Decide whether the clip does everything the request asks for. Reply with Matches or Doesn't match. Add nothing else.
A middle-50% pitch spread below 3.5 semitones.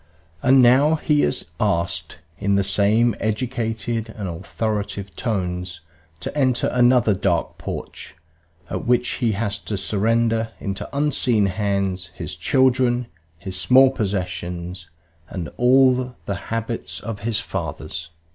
Doesn't match